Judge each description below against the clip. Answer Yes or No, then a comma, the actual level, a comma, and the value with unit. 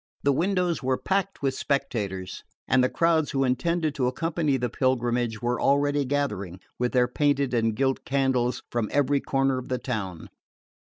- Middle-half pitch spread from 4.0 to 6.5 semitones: No, average, 2.8 semitones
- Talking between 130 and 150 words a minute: No, average, 165 wpm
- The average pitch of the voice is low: Yes, low, 130 Hz